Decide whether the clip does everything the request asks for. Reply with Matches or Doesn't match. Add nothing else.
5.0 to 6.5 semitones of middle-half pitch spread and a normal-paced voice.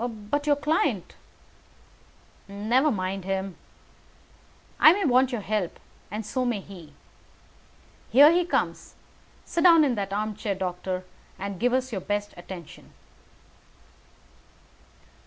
Doesn't match